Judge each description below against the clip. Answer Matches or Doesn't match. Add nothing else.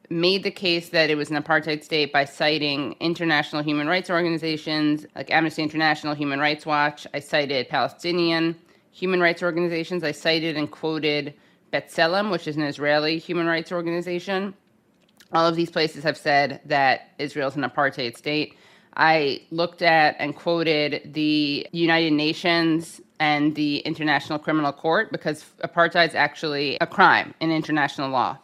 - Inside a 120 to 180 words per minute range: Matches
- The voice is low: Doesn't match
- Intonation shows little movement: Matches